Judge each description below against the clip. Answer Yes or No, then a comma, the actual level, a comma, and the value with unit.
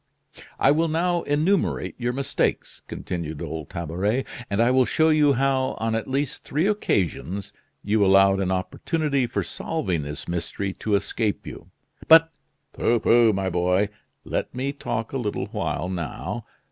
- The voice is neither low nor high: No, low, 115 Hz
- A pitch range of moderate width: No, wide, 6.8 semitones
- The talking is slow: No, average, 160 wpm